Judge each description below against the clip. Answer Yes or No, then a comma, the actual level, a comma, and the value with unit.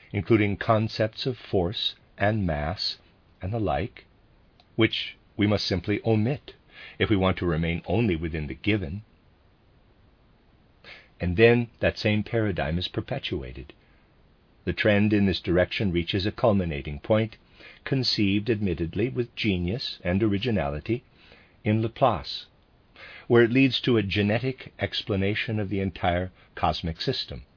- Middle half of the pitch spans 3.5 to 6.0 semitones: Yes, average, 4.0 semitones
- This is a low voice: Yes, low, 105 Hz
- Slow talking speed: Yes, slow, 130 wpm